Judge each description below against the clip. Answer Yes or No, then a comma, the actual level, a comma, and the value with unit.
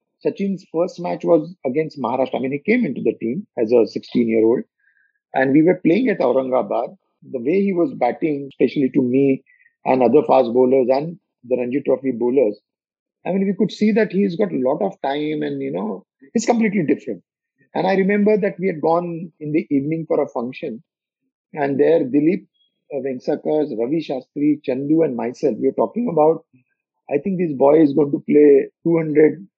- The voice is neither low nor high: Yes, medium, 160 Hz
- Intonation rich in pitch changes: Yes, wide, 6.0 semitones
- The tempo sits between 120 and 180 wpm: No, average, 190 wpm